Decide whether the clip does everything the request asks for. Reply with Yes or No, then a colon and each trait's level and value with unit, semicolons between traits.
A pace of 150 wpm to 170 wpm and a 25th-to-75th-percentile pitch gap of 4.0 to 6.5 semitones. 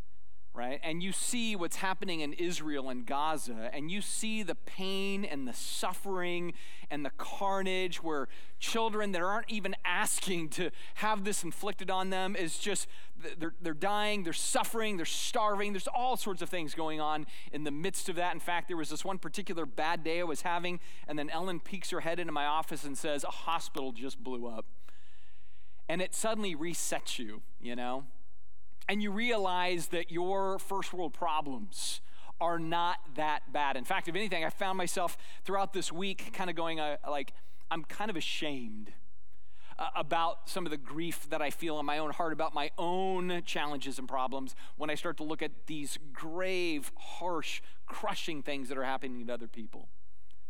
No: average, 185 wpm; average, 4.6 semitones